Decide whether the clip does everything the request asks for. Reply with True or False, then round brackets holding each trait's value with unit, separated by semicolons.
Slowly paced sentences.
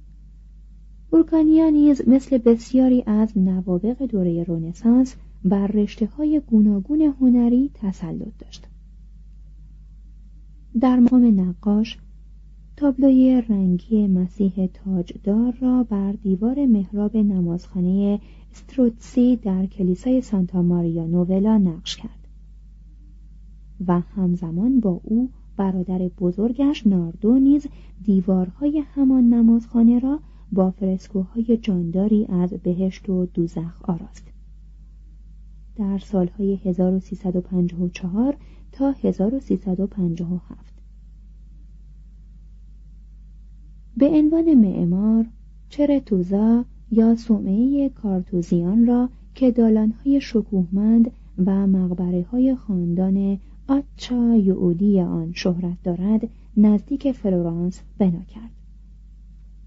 True (85 wpm)